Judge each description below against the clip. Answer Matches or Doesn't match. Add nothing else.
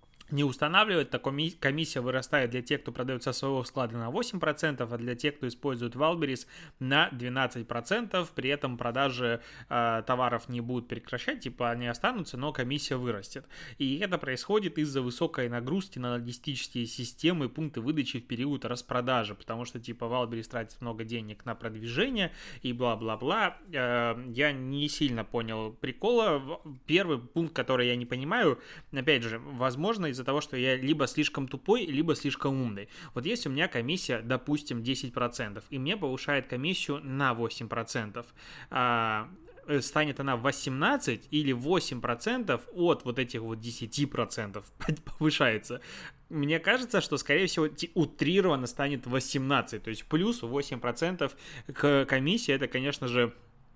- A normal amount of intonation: Matches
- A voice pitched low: Matches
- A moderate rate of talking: Matches